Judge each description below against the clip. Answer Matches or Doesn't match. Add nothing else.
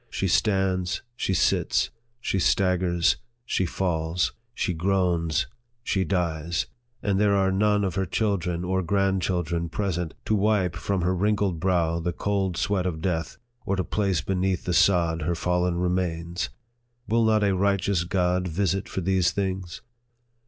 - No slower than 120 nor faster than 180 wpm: Matches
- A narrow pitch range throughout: Matches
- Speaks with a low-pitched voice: Matches